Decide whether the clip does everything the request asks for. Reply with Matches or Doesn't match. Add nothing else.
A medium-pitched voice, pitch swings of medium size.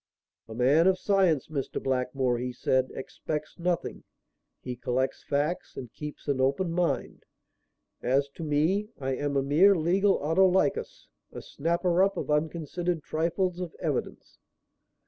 Matches